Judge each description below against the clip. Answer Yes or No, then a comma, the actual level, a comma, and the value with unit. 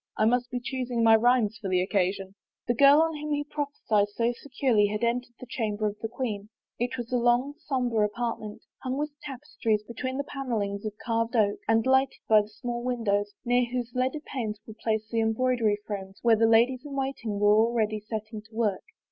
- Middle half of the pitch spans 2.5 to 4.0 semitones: Yes, average, 3.0 semitones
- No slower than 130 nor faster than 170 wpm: No, average, 200 wpm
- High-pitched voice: Yes, high, 230 Hz